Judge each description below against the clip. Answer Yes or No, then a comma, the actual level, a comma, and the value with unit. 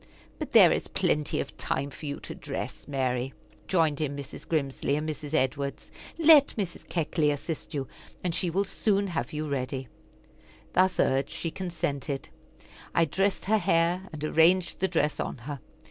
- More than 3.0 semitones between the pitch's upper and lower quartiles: Yes, average, 4.1 semitones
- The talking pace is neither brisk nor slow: Yes, average, 165 wpm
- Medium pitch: Yes, medium, 155 Hz